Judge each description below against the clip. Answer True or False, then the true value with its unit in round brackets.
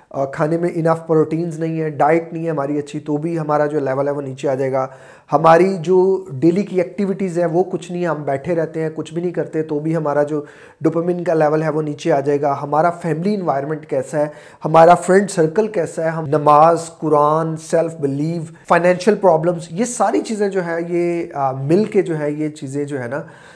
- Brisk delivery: True (215 wpm)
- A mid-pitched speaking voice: True (160 Hz)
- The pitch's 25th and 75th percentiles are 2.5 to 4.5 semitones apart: True (2.8 semitones)